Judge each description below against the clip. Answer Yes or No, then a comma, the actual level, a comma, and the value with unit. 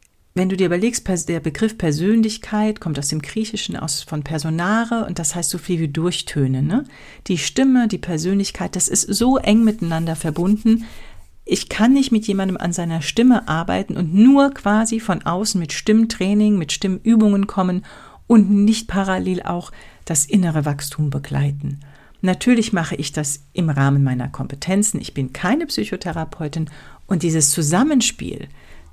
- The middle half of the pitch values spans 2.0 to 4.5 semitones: No, average, 5.2 semitones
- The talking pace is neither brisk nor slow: Yes, average, 155 wpm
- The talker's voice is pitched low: No, medium, 185 Hz